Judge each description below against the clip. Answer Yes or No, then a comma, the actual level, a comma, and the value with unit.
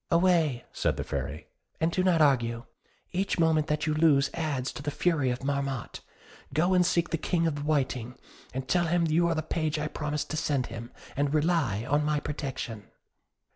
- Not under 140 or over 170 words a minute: No, average, 190 wpm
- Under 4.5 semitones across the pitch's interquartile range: Yes, average, 3.3 semitones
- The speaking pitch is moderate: Yes, medium, 150 Hz